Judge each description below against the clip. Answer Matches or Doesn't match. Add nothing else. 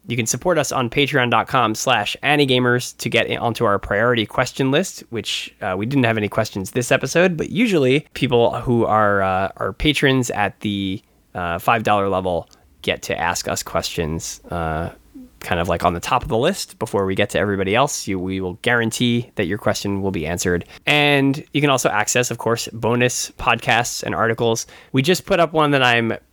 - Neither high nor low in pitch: Doesn't match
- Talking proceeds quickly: Doesn't match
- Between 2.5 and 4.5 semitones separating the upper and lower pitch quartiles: Doesn't match